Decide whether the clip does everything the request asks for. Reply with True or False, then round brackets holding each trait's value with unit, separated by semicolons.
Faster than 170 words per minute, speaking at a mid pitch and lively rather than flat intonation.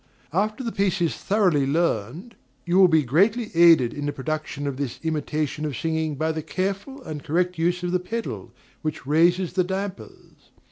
False (180 wpm; 170 Hz; 3.9 semitones)